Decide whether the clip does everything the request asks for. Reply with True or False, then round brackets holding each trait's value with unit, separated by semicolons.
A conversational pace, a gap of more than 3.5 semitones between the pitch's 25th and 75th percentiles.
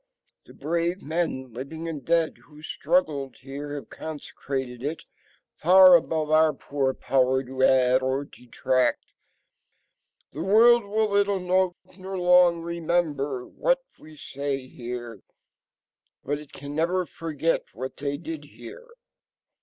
False (130 wpm; 4.7 semitones)